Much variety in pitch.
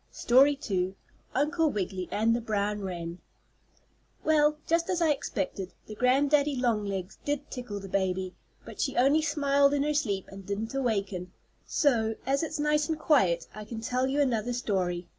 Yes: wide, 6.6 semitones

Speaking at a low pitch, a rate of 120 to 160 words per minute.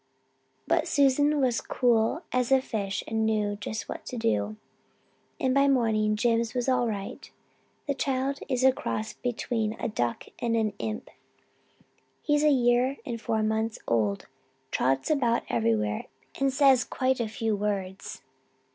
No: high, 230 Hz; average, 150 wpm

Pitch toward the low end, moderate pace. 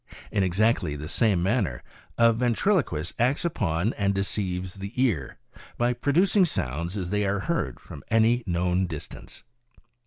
Yes: low, 100 Hz; average, 145 wpm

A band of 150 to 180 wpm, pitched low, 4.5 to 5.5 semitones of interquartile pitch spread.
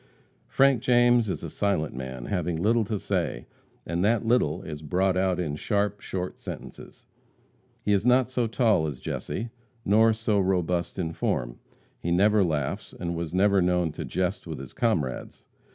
Yes: average, 170 wpm; very low, 95 Hz; average, 4.8 semitones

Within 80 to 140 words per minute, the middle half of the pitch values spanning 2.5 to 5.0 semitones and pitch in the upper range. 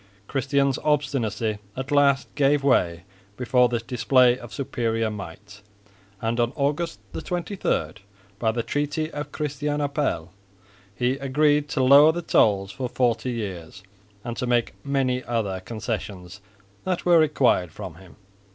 No: slow, 135 wpm; average, 4.4 semitones; low, 125 Hz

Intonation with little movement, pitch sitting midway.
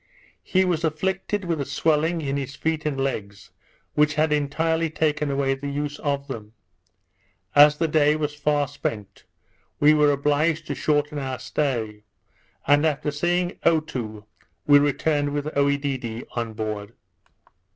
Yes: narrow, 2.2 semitones; medium, 145 Hz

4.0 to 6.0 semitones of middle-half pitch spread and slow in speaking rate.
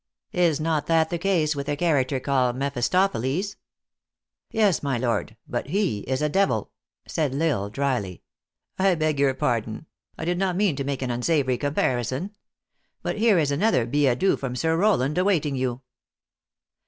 No: average, 5.1 semitones; average, 175 wpm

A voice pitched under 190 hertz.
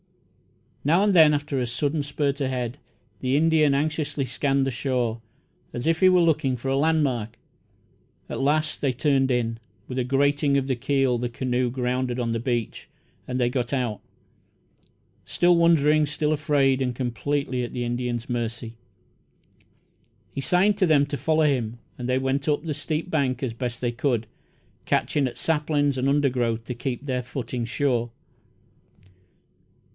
Yes: low, 135 Hz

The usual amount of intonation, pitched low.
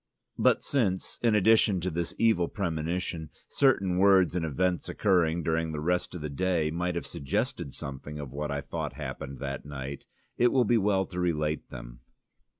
Yes: average, 3.9 semitones; very low, 85 Hz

